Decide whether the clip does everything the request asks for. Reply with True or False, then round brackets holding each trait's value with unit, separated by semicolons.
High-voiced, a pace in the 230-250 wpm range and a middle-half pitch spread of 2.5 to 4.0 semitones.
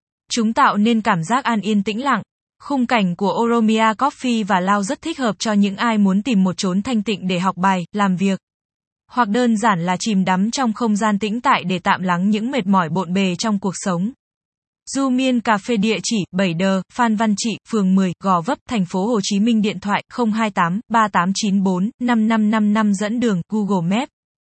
False (215 Hz; 200 wpm; 3.3 semitones)